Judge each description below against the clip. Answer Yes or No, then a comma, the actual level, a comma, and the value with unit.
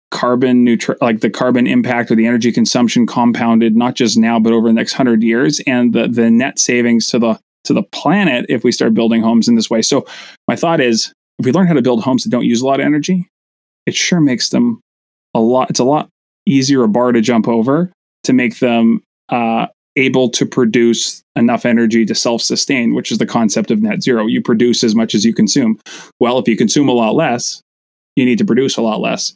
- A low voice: Yes, low, 120 Hz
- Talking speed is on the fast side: Yes, fast, 225 wpm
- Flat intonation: No, average, 4.4 semitones